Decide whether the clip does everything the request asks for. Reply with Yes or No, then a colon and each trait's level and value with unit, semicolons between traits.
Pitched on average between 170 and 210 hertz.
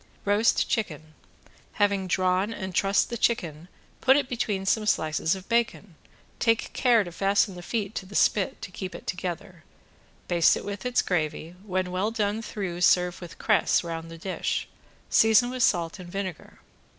Yes: high, 190 Hz